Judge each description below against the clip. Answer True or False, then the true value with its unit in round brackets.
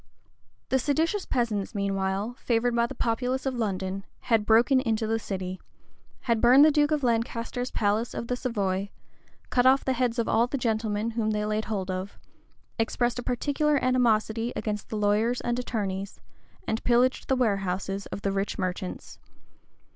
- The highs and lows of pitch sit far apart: False (3.3 semitones)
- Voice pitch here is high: True (225 Hz)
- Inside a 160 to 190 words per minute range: True (165 wpm)